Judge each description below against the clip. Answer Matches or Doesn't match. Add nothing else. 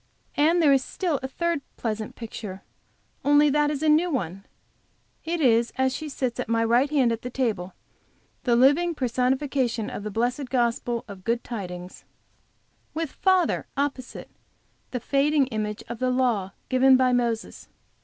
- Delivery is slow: Doesn't match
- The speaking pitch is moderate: Doesn't match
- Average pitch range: Matches